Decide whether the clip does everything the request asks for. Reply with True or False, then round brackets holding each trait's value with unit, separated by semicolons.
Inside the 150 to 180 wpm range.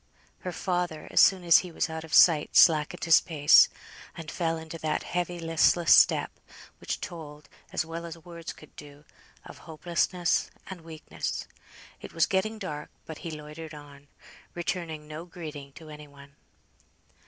True (160 wpm)